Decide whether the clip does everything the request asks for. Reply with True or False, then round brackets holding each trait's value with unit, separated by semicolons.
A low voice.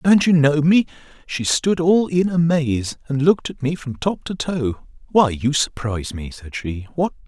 False (145 Hz)